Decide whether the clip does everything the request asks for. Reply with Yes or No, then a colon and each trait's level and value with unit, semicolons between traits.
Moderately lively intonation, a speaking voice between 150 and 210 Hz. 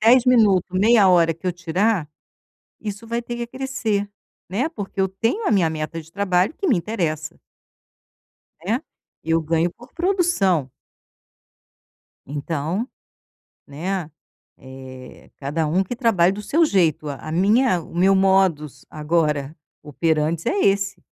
No: wide, 5.8 semitones; medium, 185 Hz